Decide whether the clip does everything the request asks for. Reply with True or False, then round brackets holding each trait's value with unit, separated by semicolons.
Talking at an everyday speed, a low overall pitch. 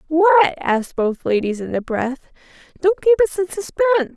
False (175 wpm; 315 Hz)